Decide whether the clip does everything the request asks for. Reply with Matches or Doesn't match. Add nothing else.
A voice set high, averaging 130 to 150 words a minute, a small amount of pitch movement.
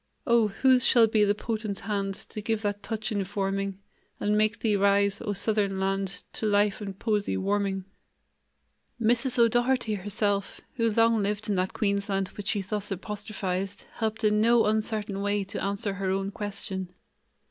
Doesn't match